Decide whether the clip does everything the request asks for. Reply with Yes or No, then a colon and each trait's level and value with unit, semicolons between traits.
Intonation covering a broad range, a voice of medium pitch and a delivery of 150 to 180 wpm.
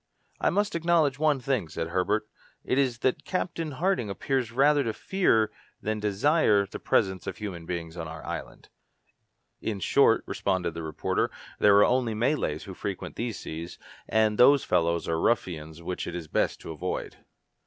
No: wide, 7.6 semitones; low, 105 Hz; average, 170 wpm